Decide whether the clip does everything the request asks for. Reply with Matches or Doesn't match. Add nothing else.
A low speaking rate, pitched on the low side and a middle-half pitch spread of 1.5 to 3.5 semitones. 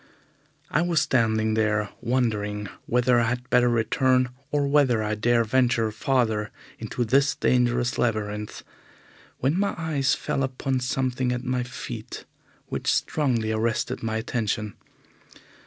Matches